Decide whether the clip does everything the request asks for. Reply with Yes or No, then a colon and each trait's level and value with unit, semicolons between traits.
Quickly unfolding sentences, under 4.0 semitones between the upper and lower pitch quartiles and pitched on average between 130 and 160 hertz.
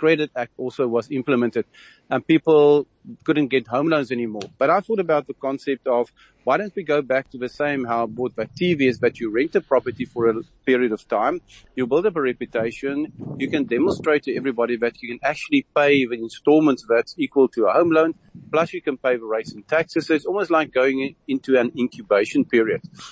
No: fast, 215 wpm; average, 4.5 semitones; low, 135 Hz